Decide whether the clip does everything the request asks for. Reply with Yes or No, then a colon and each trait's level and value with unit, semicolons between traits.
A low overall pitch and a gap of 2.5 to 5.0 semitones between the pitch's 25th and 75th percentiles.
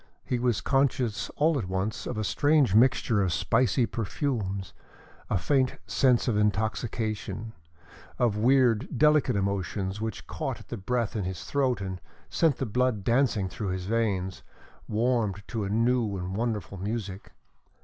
Yes: low, 110 Hz; average, 4.1 semitones